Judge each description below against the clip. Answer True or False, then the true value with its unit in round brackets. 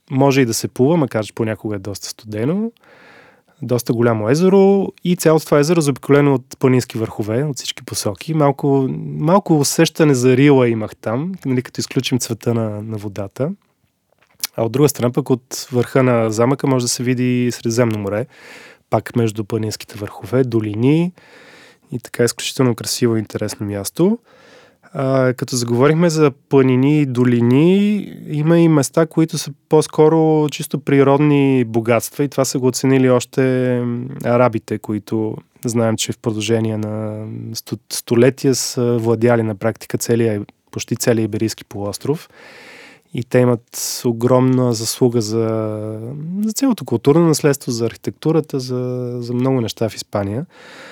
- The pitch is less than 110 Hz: False (125 Hz)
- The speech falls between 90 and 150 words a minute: True (145 wpm)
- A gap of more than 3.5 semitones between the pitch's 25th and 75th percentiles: True (4.2 semitones)